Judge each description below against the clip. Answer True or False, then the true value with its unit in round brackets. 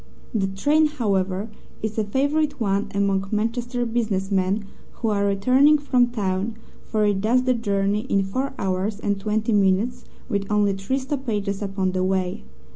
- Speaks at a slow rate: False (160 wpm)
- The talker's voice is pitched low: False (210 Hz)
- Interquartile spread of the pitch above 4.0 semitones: False (3.7 semitones)